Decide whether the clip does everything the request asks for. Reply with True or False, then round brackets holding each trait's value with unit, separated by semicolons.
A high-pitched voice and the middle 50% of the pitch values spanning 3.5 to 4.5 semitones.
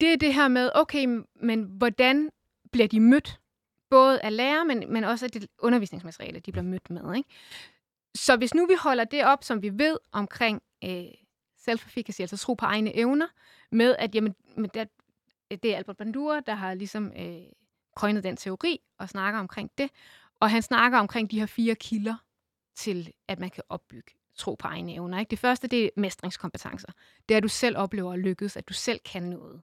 True (225 Hz; 3.9 semitones)